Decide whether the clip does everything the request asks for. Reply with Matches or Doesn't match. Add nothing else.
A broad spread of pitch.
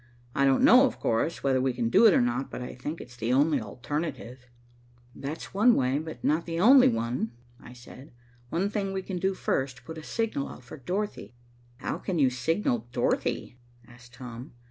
Matches